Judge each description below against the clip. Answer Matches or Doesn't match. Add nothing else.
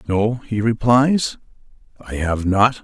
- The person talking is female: Doesn't match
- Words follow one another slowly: Matches